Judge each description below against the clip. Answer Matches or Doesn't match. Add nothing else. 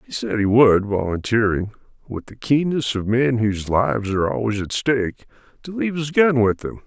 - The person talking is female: Doesn't match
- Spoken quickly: Doesn't match